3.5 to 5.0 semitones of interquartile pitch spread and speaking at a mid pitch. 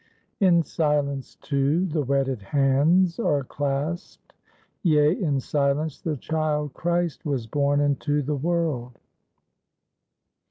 No: average, 2.8 semitones; medium, 145 Hz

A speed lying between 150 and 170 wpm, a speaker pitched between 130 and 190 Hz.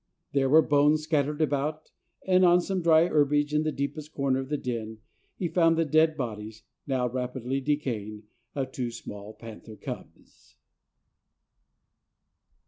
No: average, 140 wpm; medium, 140 Hz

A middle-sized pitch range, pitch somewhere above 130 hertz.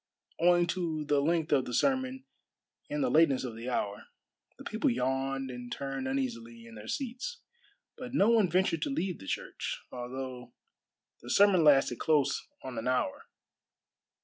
No: wide, 7.0 semitones; medium, 140 Hz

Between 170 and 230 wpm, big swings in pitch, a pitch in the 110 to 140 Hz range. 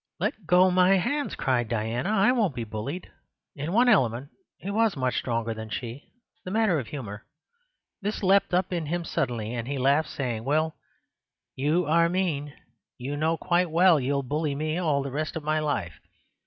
No: average, 180 wpm; wide, 6.0 semitones; medium, 155 Hz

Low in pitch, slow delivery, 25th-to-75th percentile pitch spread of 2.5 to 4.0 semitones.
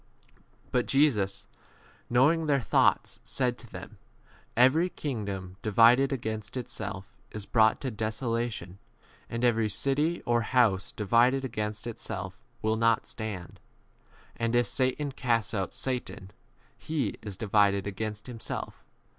Yes: low, 115 Hz; slow, 130 wpm; average, 3.5 semitones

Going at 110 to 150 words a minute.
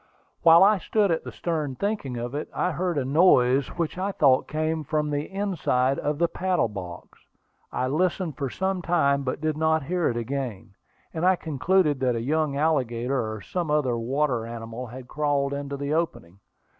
No: average, 185 wpm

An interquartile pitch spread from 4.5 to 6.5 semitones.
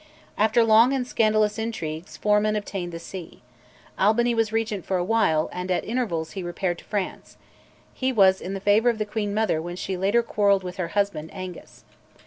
No: average, 3.5 semitones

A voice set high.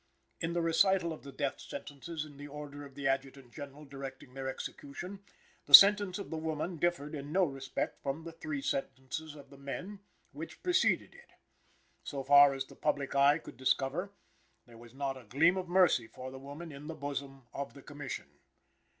No: medium, 145 Hz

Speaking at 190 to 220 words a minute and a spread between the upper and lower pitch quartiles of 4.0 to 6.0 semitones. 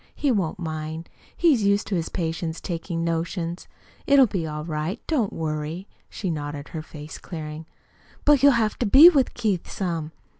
No: average, 165 wpm; average, 5.1 semitones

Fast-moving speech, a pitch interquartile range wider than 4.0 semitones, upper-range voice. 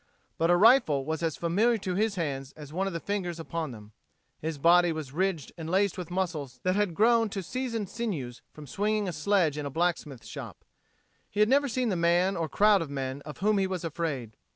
No: fast, 220 wpm; average, 5.0 semitones; medium, 175 Hz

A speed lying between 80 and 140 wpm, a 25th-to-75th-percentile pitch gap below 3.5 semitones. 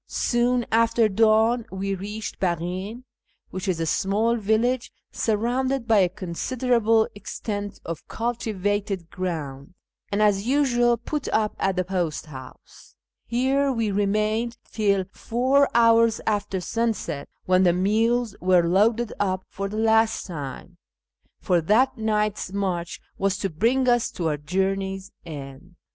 No: slow, 135 wpm; average, 3.8 semitones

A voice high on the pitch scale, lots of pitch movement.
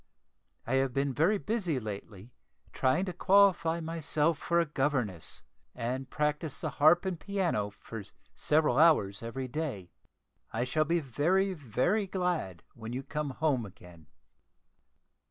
No: medium, 150 Hz; wide, 5.8 semitones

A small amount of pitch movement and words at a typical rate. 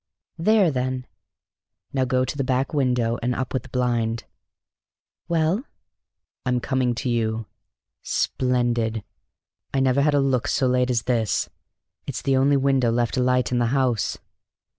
Yes: narrow, 2.0 semitones; average, 150 wpm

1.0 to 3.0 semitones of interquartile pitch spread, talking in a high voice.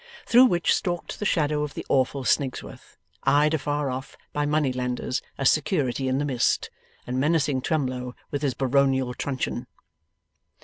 No: narrow, 2.6 semitones; medium, 140 Hz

